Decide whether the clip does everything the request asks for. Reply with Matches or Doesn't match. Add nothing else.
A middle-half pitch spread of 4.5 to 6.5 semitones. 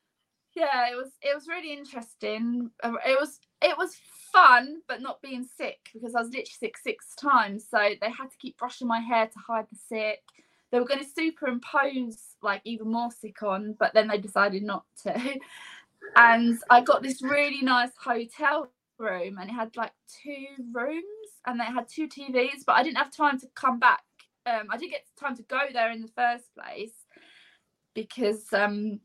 Doesn't match